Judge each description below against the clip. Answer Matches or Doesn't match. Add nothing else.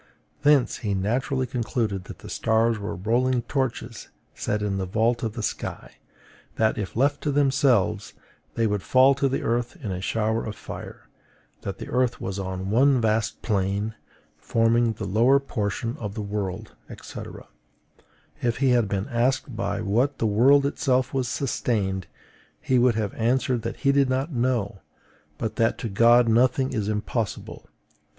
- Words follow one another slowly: Doesn't match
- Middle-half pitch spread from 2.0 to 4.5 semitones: Matches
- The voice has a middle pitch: Doesn't match